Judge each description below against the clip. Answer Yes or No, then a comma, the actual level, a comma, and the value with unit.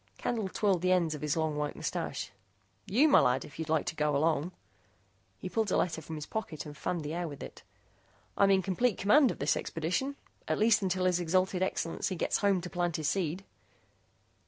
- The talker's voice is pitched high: No, medium, 175 Hz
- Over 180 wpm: Yes, fast, 205 wpm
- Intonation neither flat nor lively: Yes, average, 3.9 semitones